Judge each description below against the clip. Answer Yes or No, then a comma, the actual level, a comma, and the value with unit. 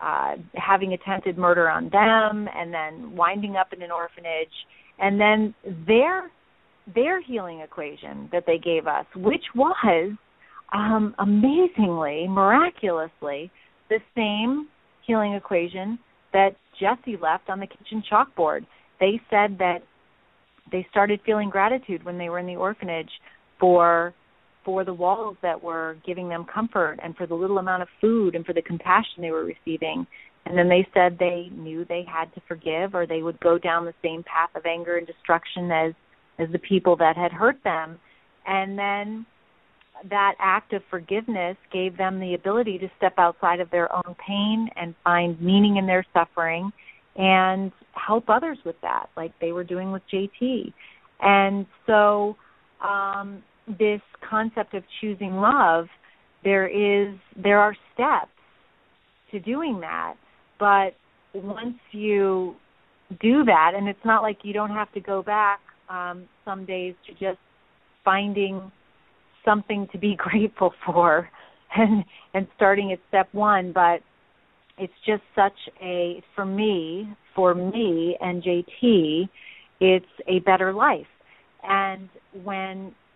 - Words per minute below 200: Yes, average, 150 wpm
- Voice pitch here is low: No, high, 190 Hz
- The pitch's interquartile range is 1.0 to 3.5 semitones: Yes, average, 2.9 semitones